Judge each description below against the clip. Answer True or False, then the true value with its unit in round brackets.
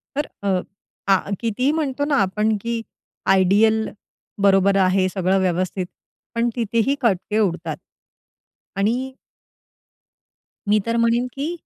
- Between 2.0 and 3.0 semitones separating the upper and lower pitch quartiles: False (3.7 semitones)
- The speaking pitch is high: True (220 Hz)